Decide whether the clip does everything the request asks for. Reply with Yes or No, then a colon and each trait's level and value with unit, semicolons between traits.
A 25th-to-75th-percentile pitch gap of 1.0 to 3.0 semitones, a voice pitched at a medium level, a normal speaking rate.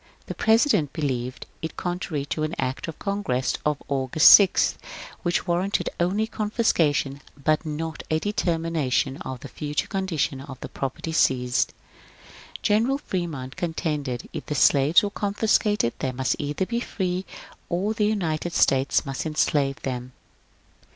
No: wide, 5.5 semitones; medium, 155 Hz; average, 145 wpm